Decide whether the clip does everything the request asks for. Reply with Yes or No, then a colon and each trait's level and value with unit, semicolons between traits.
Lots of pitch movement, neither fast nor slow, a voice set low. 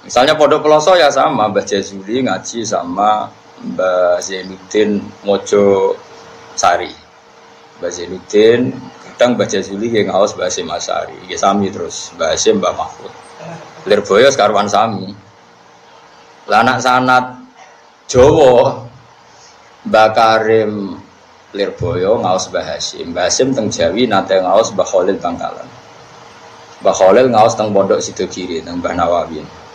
Yes: wide, 5.7 semitones; average, 120 wpm; low, 110 Hz